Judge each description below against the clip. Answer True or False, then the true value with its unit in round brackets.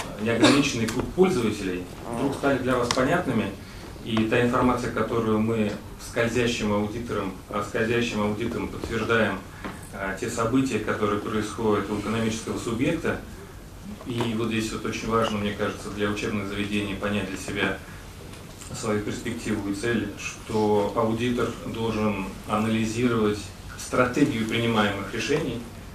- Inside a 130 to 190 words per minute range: False (115 wpm)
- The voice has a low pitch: True (110 Hz)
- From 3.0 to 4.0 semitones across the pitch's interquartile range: False (2.4 semitones)